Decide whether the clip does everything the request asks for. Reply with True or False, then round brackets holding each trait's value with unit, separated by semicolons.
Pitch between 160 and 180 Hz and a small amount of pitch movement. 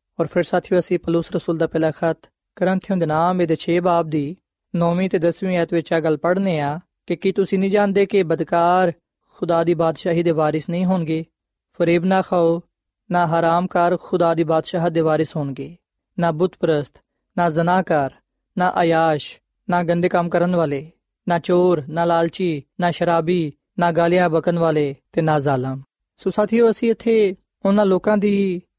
True (170 Hz; 1.9 semitones)